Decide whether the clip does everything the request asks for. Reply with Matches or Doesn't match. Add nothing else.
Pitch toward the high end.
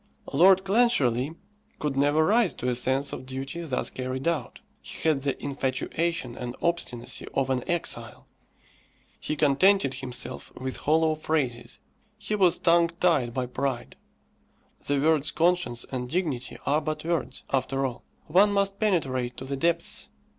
Doesn't match